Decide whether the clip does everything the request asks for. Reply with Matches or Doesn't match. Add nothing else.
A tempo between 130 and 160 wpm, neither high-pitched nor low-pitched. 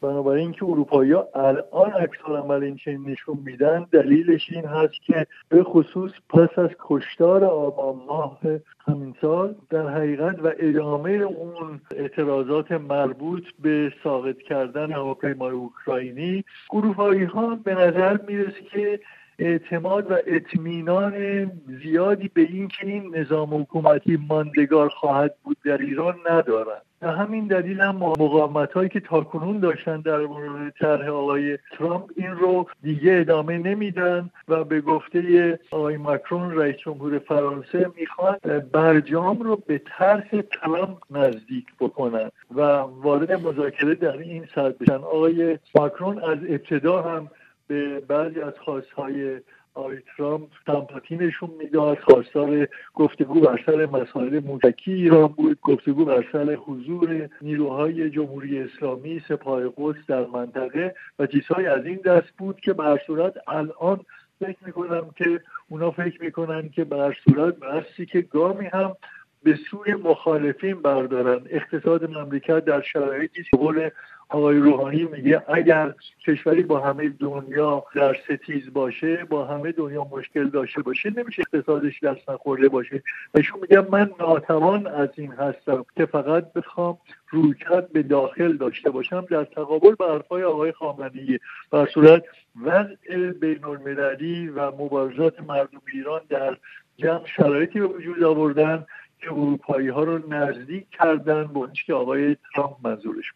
Matches